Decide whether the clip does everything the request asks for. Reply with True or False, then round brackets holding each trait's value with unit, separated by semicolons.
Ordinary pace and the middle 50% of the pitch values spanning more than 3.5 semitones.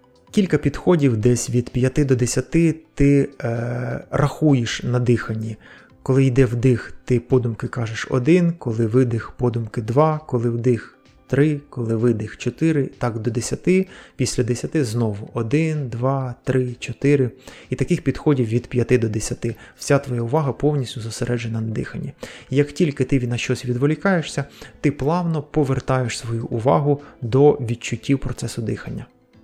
False (140 wpm; 3.1 semitones)